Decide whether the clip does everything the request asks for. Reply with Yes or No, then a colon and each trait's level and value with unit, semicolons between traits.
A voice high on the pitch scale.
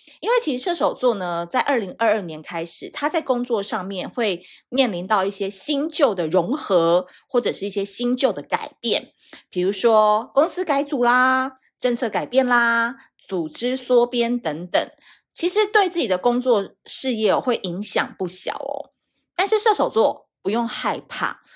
Yes: high, 245 Hz